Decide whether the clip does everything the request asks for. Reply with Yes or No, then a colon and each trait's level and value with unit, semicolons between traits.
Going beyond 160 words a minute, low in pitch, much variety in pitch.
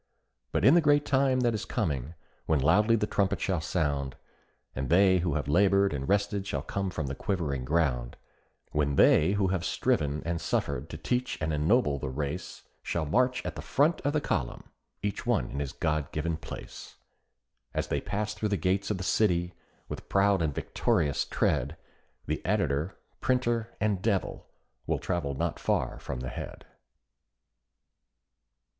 Yes: average, 170 wpm; very low, 85 Hz; wide, 5.9 semitones